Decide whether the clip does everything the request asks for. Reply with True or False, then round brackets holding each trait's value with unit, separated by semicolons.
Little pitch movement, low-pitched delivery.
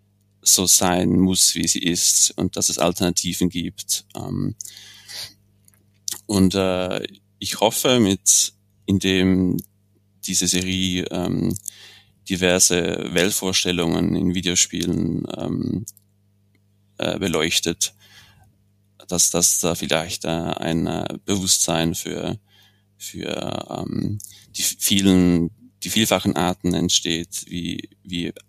True (2.0 semitones; 95 Hz)